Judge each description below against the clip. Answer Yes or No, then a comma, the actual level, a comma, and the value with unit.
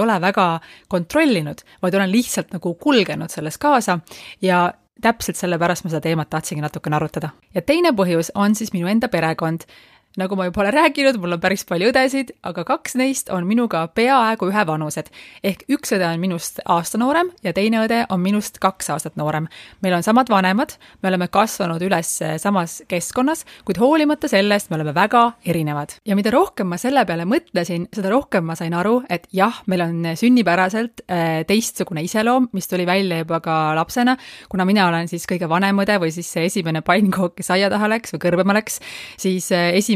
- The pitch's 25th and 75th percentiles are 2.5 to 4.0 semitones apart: No, average, 4.6 semitones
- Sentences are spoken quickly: No, average, 185 wpm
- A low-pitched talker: No, high, 190 Hz